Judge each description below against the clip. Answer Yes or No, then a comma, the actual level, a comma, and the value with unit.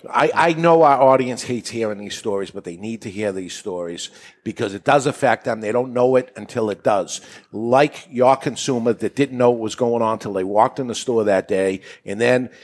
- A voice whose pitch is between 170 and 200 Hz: No, low, 120 Hz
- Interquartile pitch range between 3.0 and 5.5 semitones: Yes, average, 4.1 semitones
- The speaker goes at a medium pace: No, fast, 235 wpm